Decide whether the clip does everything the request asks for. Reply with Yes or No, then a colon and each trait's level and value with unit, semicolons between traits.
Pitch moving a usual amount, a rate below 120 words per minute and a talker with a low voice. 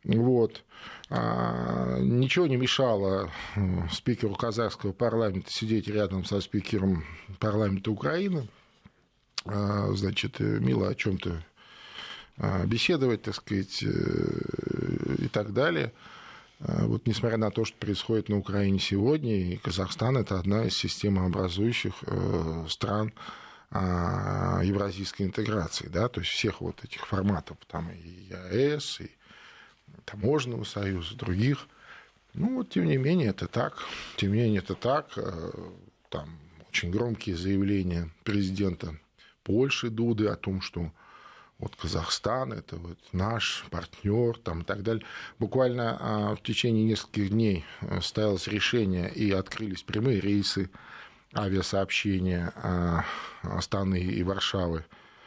Yes: average, 3.6 semitones; slow, 110 wpm; low, 100 Hz